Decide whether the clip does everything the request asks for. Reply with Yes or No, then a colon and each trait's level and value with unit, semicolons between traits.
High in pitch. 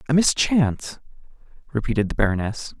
No: low, 125 Hz